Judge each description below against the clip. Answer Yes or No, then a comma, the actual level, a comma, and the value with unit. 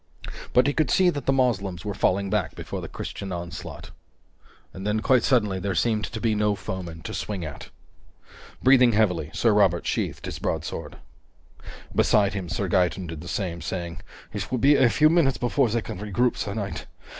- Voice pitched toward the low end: Yes, low, 105 Hz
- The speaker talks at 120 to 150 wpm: No, average, 190 wpm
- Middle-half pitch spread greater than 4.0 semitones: Yes, average, 4.9 semitones